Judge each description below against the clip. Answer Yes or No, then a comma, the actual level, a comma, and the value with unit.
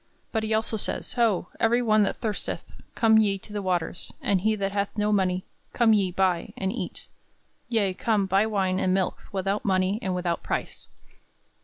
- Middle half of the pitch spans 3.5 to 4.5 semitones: No, narrow, 2.6 semitones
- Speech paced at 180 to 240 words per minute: Yes, average, 185 wpm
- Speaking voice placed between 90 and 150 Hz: No, high, 200 Hz